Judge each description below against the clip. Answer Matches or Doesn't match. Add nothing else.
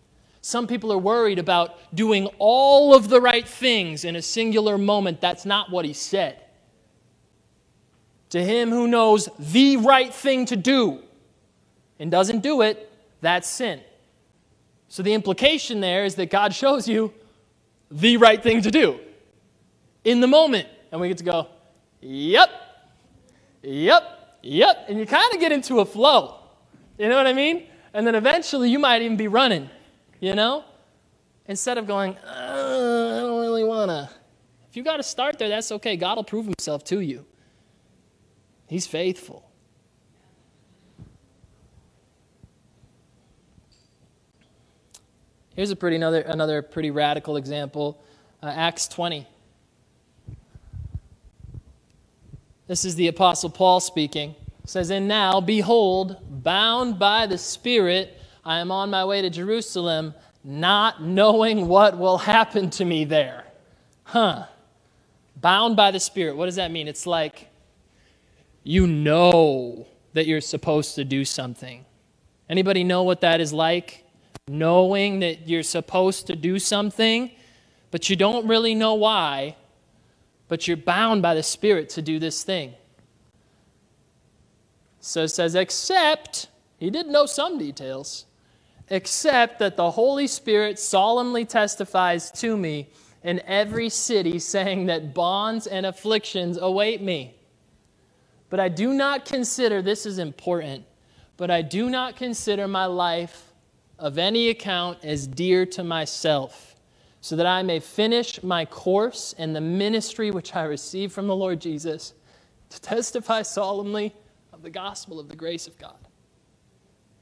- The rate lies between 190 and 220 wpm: Doesn't match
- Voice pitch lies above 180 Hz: Matches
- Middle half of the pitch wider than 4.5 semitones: Matches